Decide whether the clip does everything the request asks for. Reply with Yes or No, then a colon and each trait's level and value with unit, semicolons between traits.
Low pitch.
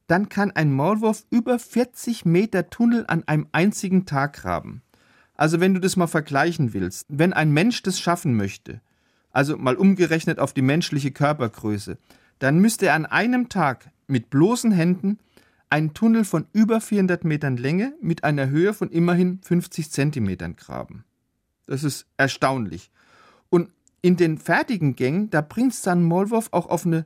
No: medium, 170 Hz